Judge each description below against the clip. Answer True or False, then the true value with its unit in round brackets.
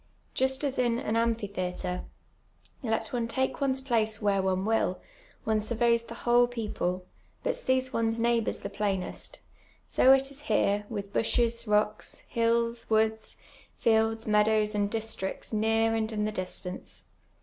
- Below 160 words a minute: True (150 wpm)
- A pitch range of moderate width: False (2.0 semitones)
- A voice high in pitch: True (225 Hz)